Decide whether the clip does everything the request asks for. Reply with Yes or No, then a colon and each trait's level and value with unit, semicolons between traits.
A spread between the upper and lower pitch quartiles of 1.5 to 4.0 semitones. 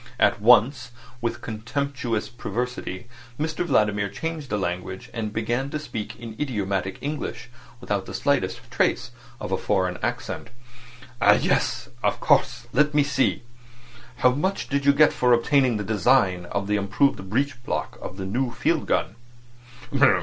No: average, 5.3 semitones